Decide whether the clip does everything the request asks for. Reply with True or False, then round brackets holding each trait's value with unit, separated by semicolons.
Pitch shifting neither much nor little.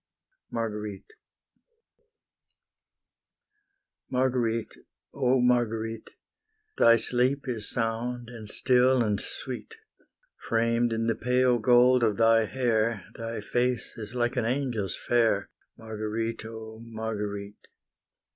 False (1.9 semitones)